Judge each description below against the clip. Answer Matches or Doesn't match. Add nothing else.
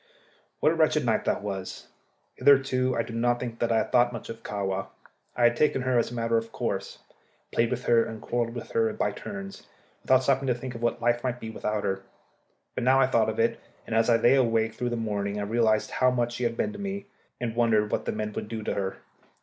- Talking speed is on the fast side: Matches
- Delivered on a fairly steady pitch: Matches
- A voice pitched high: Doesn't match